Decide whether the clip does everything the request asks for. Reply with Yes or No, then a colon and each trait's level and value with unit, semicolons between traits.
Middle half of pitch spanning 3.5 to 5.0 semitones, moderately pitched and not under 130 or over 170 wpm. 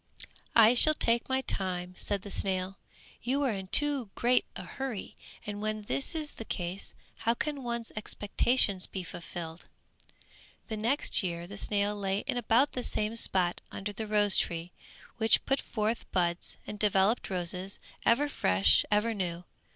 No: average, 4.0 semitones; high, 210 Hz; average, 160 wpm